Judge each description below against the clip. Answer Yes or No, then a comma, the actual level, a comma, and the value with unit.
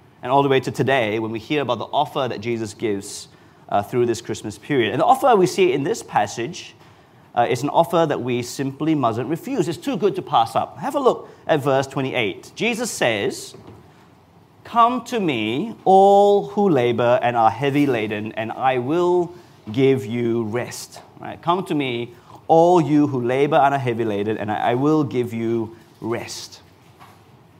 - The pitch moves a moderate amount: No, wide, 5.8 semitones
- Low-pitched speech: Yes, low, 130 Hz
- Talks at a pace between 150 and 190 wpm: Yes, average, 185 wpm